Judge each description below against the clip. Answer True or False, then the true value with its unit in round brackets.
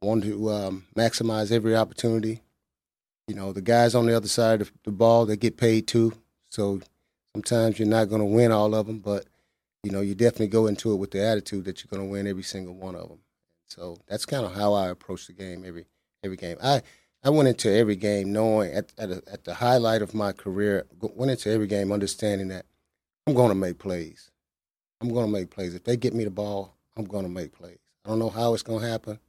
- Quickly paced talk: True (235 wpm)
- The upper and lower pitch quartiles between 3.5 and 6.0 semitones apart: False (2.8 semitones)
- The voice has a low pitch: True (105 Hz)